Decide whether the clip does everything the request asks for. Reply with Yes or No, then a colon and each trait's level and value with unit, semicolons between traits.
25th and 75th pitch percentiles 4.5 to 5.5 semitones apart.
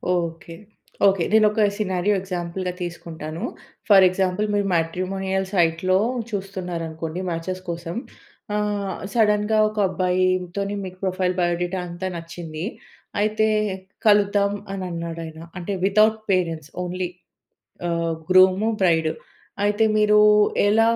No: average, 3.0 semitones